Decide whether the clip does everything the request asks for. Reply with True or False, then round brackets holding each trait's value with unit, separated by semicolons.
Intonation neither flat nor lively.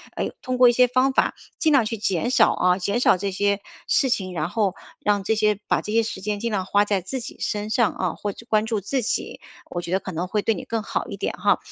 True (3.3 semitones)